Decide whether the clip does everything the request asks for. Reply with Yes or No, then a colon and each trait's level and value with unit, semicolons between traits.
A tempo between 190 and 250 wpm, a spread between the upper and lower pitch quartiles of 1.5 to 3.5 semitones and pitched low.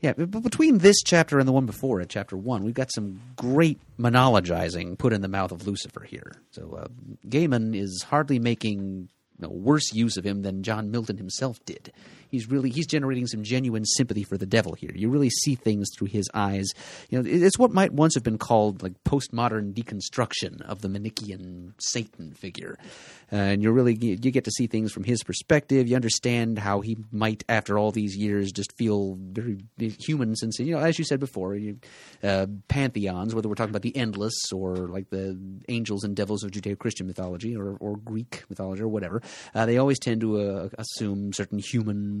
No: average, 200 wpm; average, 4.0 semitones; low, 110 Hz